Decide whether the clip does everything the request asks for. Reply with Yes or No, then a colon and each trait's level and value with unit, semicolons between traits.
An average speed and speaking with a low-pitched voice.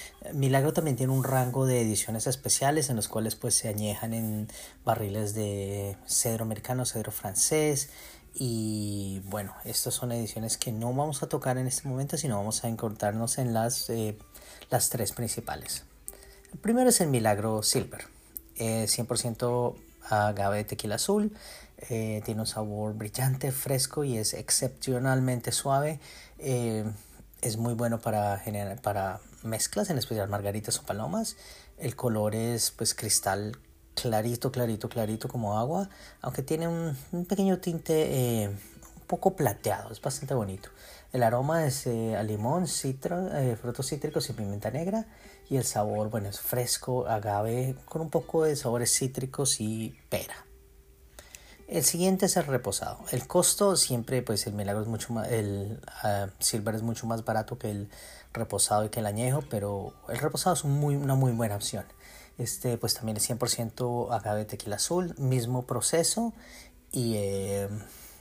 Yes: average, 160 wpm; low, 120 Hz